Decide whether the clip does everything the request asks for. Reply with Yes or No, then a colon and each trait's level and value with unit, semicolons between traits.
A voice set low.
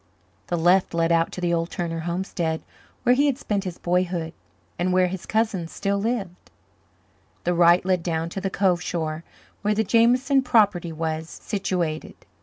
No: medium, 180 Hz